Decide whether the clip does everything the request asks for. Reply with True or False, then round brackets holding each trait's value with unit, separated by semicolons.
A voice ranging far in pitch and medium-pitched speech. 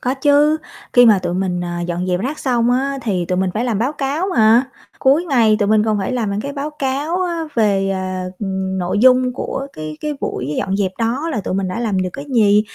False (6.1 semitones; 225 Hz)